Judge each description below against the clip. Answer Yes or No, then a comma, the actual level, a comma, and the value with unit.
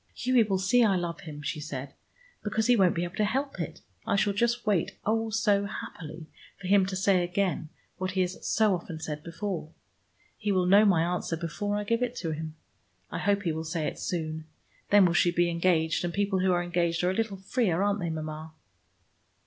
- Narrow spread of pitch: No, average, 3.6 semitones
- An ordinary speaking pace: No, fast, 215 wpm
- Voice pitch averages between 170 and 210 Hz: Yes, medium, 185 Hz